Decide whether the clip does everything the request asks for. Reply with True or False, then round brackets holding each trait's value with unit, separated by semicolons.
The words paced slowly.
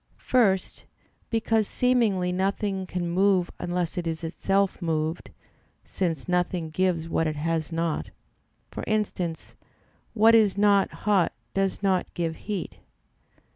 True (125 wpm)